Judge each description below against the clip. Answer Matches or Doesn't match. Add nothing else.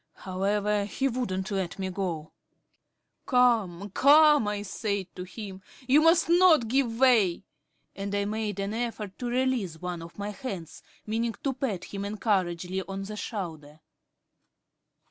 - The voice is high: Matches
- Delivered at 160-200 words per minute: Doesn't match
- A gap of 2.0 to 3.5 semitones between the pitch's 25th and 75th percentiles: Doesn't match